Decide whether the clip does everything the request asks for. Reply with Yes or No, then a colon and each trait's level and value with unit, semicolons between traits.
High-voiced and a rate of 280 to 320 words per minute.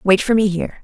Yes: high, 200 Hz; fast, 285 wpm